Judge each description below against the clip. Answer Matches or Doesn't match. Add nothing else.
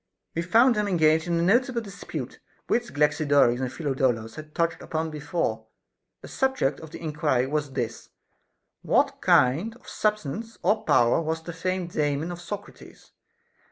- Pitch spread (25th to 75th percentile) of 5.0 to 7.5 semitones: Matches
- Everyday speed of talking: Matches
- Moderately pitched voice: Matches